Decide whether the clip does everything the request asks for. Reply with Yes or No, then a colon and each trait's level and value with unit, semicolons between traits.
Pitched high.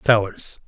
No: low, 105 Hz